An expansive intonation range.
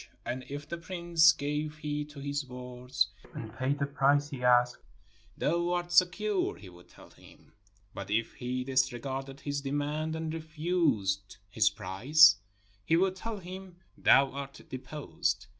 No: average, 4.3 semitones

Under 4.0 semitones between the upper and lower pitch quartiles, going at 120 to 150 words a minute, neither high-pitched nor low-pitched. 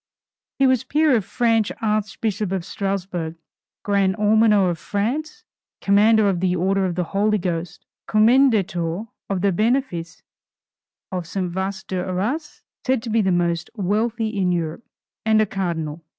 No: average, 3.5 semitones; average, 145 wpm; high, 200 Hz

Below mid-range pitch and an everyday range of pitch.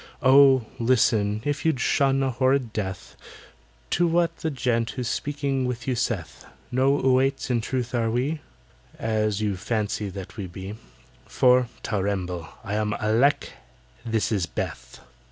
Yes: low, 120 Hz; average, 4.0 semitones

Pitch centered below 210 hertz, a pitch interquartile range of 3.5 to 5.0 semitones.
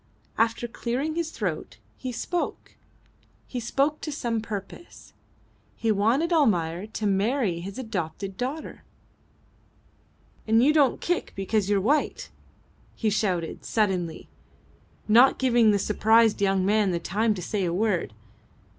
No: high, 220 Hz; average, 4.3 semitones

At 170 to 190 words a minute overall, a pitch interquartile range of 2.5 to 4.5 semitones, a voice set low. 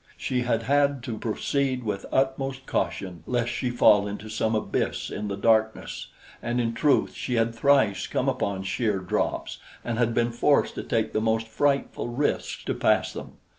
Yes: average, 175 wpm; average, 3.0 semitones; low, 115 Hz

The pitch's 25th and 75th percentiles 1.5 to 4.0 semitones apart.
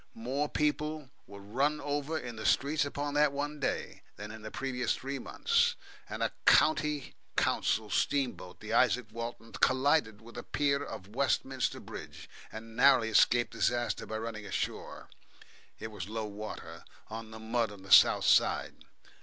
No: average, 4.6 semitones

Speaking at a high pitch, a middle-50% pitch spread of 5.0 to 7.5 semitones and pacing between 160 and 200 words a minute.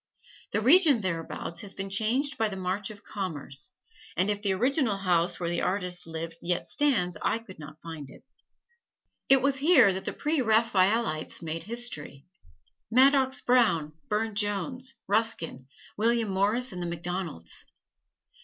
No: high, 200 Hz; wide, 5.5 semitones; average, 145 wpm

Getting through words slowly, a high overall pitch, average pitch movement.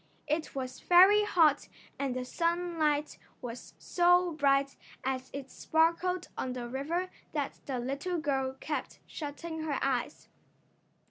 Yes: slow, 130 wpm; very high, 295 Hz; average, 4.2 semitones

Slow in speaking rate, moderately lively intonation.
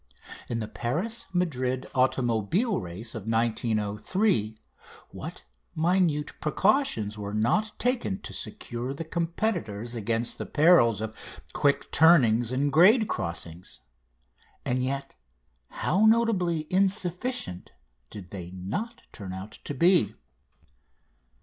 No: slow, 110 wpm; wide, 8.8 semitones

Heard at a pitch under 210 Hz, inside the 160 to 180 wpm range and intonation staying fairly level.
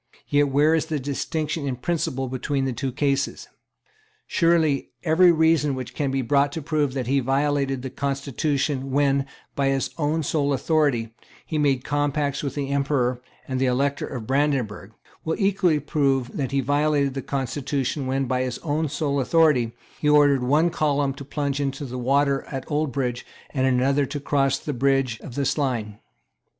Yes: medium, 140 Hz; average, 170 wpm; narrow, 1.9 semitones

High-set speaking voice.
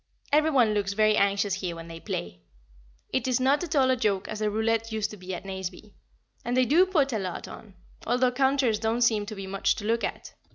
Yes: high, 220 Hz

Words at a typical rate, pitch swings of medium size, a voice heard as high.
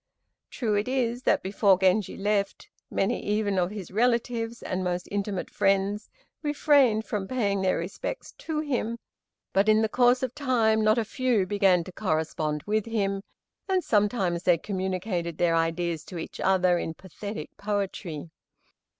Yes: average, 155 wpm; average, 3.7 semitones; high, 200 Hz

